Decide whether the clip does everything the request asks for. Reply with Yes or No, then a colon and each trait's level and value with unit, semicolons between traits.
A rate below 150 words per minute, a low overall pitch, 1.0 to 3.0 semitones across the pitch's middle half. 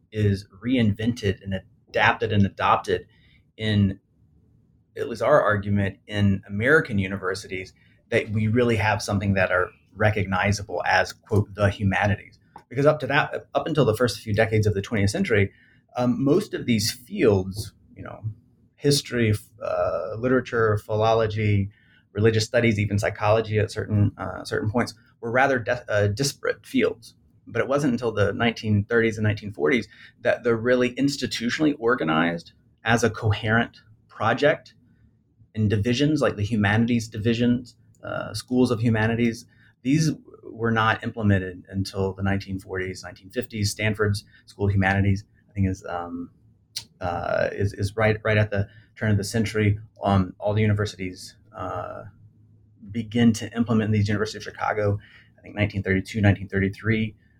Yes: average, 140 wpm; low, 110 Hz; average, 2.7 semitones